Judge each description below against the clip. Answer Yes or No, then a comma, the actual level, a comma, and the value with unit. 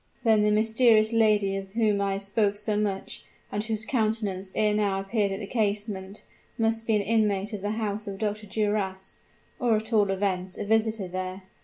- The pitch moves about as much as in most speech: No, narrow, 1.9 semitones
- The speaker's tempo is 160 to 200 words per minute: Yes, average, 190 wpm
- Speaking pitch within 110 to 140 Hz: No, high, 210 Hz